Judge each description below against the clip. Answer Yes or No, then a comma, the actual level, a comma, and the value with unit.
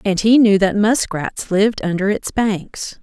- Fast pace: No, average, 180 wpm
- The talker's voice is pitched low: No, high, 200 Hz